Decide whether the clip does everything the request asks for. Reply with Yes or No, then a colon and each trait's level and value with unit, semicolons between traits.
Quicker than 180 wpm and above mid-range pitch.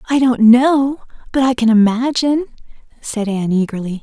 No: average, 150 wpm; high, 240 Hz